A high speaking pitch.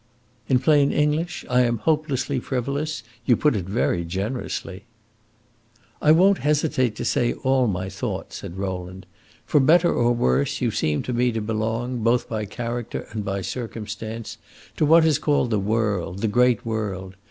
No: low, 120 Hz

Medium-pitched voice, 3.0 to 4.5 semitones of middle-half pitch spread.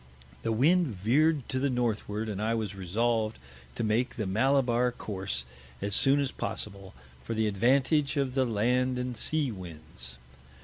No: low, 115 Hz; average, 4.1 semitones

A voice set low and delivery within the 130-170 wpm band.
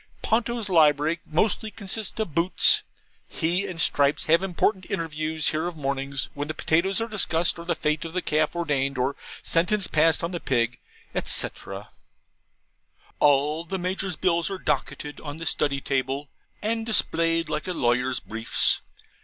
No: medium, 165 Hz; average, 155 wpm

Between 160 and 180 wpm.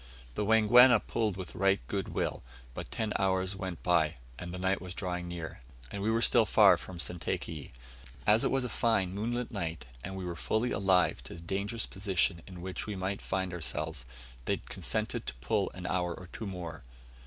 No: average, 190 wpm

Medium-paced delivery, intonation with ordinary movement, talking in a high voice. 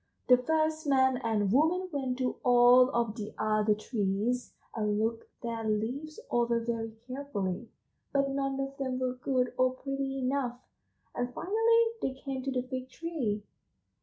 Yes: average, 155 wpm; average, 3.0 semitones; very high, 255 Hz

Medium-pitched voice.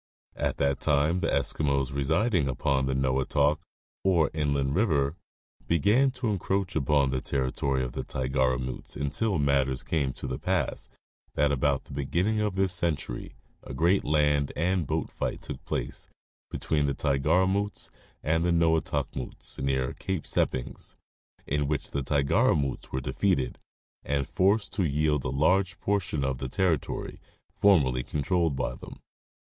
No: very low, 75 Hz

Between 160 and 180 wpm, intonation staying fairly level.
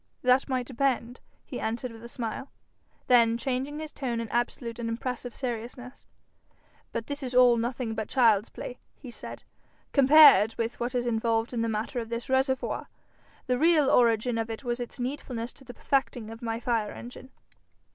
Yes: average, 175 wpm; narrow, 2.1 semitones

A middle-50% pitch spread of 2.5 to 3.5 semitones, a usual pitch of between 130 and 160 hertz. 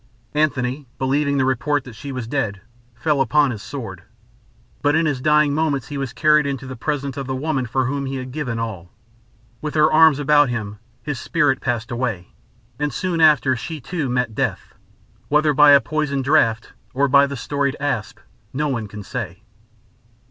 Yes: average, 3.1 semitones; medium, 140 Hz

